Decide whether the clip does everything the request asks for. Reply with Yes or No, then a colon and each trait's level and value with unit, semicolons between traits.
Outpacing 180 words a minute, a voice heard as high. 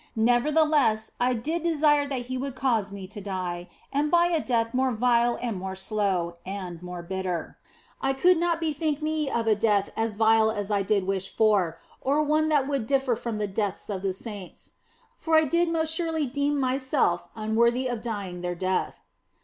Yes: average, 190 wpm; high, 235 Hz